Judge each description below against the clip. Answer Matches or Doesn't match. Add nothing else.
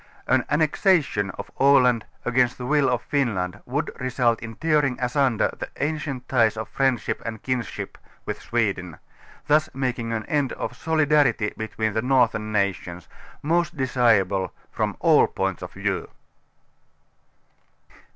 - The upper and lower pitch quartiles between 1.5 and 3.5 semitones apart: Doesn't match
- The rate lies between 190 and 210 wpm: Doesn't match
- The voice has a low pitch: Matches